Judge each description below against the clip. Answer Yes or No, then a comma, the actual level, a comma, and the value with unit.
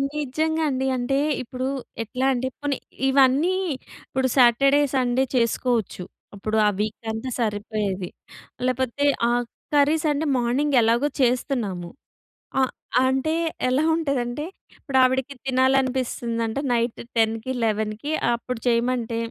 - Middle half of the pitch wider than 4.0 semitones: No, average, 2.8 semitones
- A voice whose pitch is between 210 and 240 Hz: No, very high, 255 Hz